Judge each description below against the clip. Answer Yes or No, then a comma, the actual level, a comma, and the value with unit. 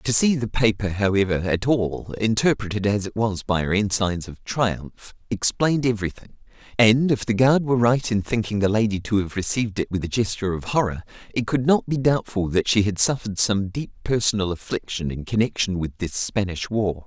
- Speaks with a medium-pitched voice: No, low, 105 Hz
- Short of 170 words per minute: No, average, 195 wpm